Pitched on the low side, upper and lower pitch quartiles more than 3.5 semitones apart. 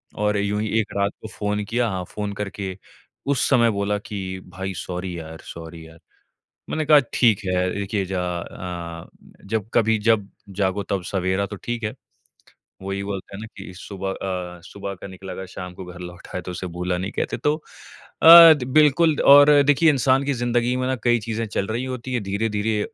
Yes: low, 100 Hz; average, 4.0 semitones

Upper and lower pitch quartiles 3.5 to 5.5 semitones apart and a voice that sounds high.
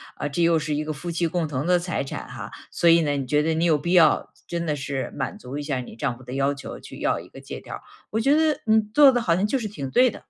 No: average, 4.1 semitones; medium, 160 Hz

